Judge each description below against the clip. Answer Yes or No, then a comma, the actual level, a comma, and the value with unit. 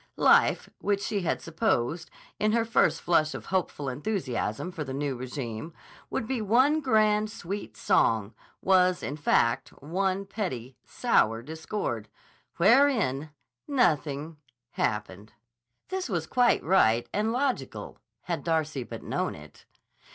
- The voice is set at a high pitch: No, medium, 165 Hz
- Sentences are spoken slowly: Yes, slow, 125 wpm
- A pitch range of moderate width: No, wide, 8.2 semitones